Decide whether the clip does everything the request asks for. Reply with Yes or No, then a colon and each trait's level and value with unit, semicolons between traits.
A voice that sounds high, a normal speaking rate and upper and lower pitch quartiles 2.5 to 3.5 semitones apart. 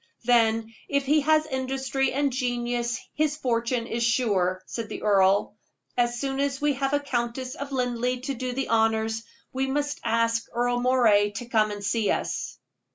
Yes: high, 245 Hz; average, 170 wpm; average, 2.9 semitones